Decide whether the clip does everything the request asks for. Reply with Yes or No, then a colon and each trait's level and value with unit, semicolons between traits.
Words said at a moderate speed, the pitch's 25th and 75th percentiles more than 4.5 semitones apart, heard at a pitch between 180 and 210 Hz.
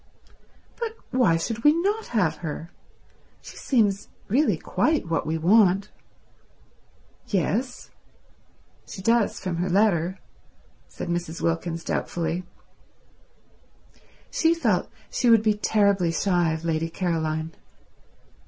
No: slow, 105 wpm; wide, 5.5 semitones; medium, 185 Hz